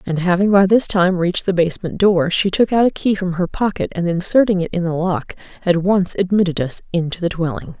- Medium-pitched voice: Yes, medium, 180 Hz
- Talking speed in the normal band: No, fast, 230 wpm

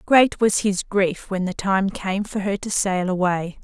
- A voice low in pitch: No, high, 195 Hz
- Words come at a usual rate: No, fast, 215 wpm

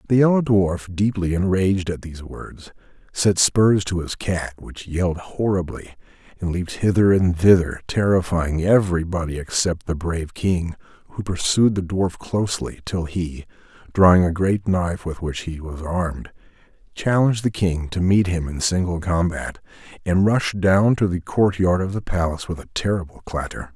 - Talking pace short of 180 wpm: Yes, average, 160 wpm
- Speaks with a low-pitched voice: Yes, very low, 90 Hz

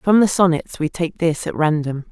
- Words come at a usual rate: No, fast, 225 wpm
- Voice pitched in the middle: Yes, medium, 165 Hz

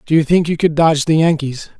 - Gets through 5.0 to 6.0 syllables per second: No, 6.3 syllables/s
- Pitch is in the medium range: Yes, medium, 155 Hz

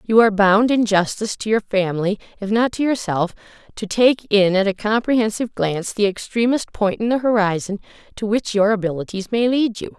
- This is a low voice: No, high, 210 Hz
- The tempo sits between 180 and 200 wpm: Yes, average, 190 wpm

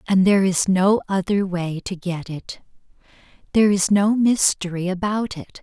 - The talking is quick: No, average, 160 wpm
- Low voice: No, high, 190 Hz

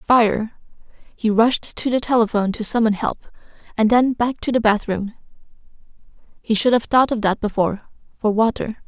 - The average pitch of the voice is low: No, high, 225 Hz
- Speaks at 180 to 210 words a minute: No, average, 150 wpm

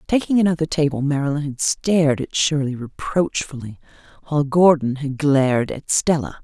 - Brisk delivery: No, average, 140 wpm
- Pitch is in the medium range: Yes, medium, 145 Hz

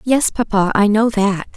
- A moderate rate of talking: Yes, average, 190 wpm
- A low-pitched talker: No, high, 215 Hz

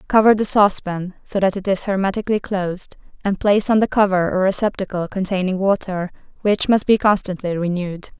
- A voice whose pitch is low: No, high, 195 Hz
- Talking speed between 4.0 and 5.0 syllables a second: No, 5.9 syllables/s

